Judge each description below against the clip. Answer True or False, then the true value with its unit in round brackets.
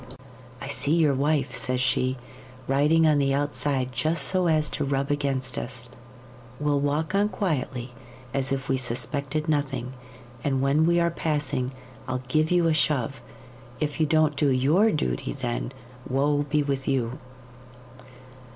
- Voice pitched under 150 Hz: True (140 Hz)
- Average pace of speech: True (150 wpm)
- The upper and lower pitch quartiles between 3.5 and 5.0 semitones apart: False (2.8 semitones)